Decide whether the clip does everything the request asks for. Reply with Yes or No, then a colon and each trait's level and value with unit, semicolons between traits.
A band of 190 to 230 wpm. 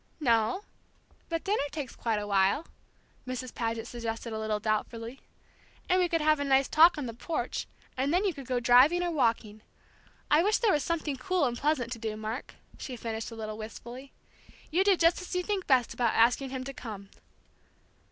Yes: average, 195 wpm